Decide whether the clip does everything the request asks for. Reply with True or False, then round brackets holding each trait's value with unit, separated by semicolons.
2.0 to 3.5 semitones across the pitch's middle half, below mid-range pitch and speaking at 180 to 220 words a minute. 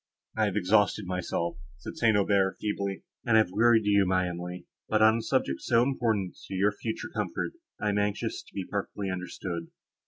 True (2.9 semitones; 100 Hz; 185 wpm)